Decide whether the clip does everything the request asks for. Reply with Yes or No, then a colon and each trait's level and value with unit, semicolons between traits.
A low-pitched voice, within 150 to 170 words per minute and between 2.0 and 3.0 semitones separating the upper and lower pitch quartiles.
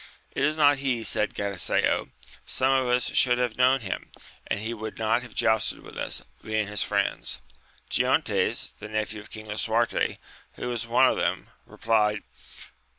Yes: low, 110 Hz; average, 165 wpm; average, 2.7 semitones